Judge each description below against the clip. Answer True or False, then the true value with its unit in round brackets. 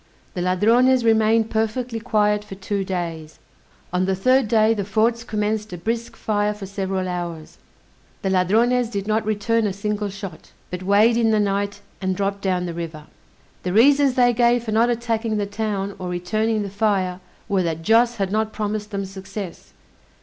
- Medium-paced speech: True (180 wpm)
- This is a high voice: True (210 Hz)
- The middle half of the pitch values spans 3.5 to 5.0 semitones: False (2.8 semitones)